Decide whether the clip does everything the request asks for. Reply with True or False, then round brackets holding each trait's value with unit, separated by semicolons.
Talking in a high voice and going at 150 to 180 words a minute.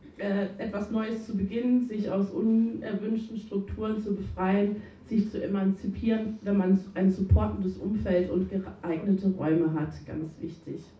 False (200 Hz; 130 wpm)